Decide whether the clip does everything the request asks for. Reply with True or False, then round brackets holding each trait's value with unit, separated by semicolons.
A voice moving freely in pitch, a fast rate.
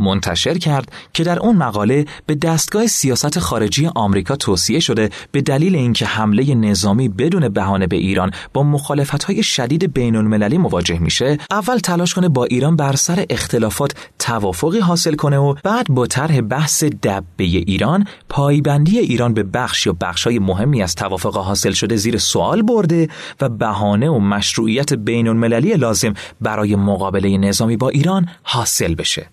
True (6.8 semitones; 160 wpm)